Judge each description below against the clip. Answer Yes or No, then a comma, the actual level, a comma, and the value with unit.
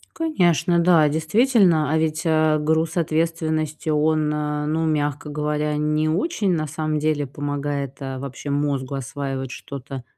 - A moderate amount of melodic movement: No, narrow, 1.8 semitones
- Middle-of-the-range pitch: Yes, medium, 155 Hz